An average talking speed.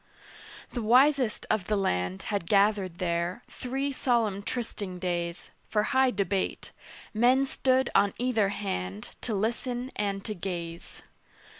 No: slow, 130 wpm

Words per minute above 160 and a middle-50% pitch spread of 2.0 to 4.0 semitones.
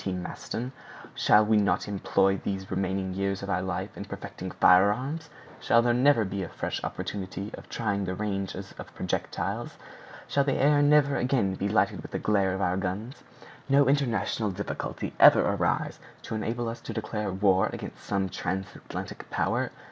Yes: average, 170 wpm; average, 3.7 semitones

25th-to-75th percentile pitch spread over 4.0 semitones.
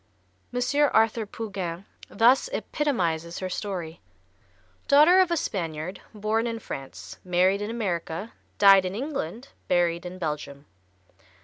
Yes: wide, 5.4 semitones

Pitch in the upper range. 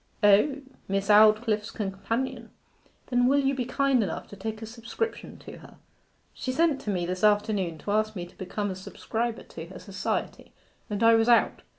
Yes: high, 215 Hz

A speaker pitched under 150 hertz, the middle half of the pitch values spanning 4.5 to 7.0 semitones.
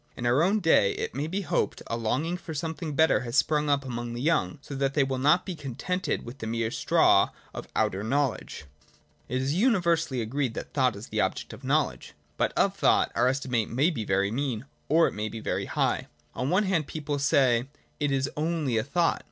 Yes: medium, 140 Hz; average, 5.1 semitones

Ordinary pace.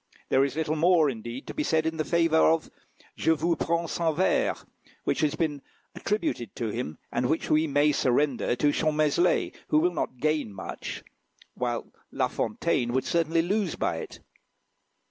Yes: average, 165 wpm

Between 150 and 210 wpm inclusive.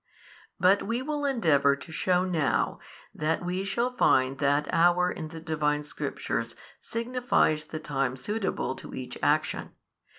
No: average, 140 wpm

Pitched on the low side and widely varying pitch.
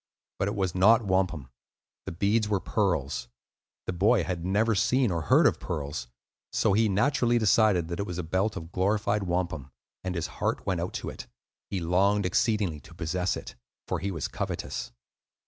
No: very low, 95 Hz; average, 3.5 semitones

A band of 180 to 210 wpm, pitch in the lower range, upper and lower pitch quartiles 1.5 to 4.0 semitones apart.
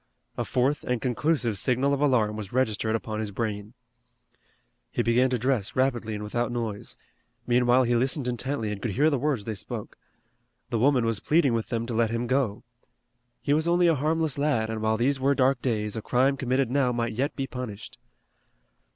Yes: average, 195 wpm; low, 125 Hz; average, 3.5 semitones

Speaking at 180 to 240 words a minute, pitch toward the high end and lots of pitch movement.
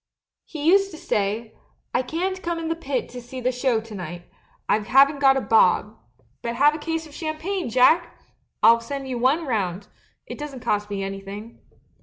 Yes: average, 200 wpm; very high, 255 Hz; wide, 6.2 semitones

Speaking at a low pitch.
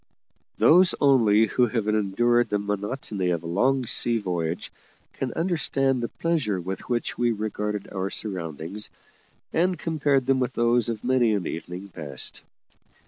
Yes: low, 110 Hz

